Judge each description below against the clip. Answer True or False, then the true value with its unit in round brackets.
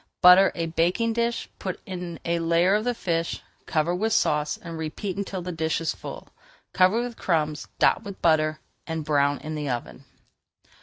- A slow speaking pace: False (175 wpm)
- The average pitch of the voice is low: False (170 Hz)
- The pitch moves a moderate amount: True (3.5 semitones)